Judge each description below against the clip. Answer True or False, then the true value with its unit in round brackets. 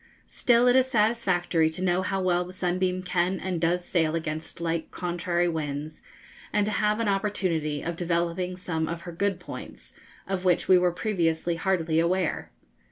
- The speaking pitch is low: False (180 Hz)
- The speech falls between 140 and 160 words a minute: False (170 wpm)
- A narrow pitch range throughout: True (2.2 semitones)